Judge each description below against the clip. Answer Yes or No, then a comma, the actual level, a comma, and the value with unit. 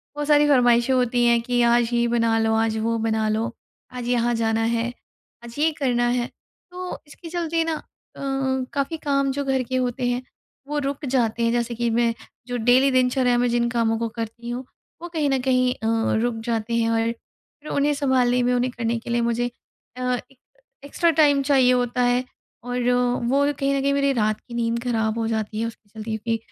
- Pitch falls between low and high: No, high, 245 Hz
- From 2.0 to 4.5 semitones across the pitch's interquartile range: Yes, narrow, 2.6 semitones